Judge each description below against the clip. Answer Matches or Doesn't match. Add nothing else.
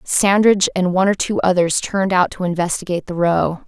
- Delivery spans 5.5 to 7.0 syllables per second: Matches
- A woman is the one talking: Matches